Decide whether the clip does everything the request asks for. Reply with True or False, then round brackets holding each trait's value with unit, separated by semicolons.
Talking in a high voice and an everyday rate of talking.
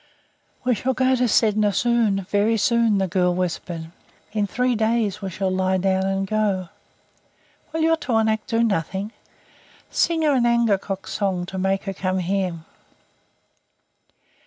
True (205 Hz; 145 wpm)